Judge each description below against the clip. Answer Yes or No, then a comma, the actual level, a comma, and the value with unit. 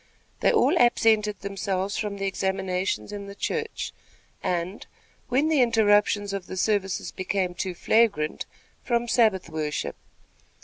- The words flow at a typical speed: No, slow, 130 wpm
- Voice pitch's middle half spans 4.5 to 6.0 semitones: No, average, 2.9 semitones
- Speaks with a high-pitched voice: Yes, high, 200 Hz